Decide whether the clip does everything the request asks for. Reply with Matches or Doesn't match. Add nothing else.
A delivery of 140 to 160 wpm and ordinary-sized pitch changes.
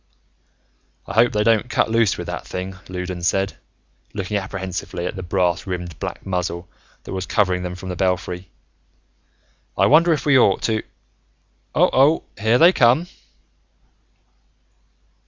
Matches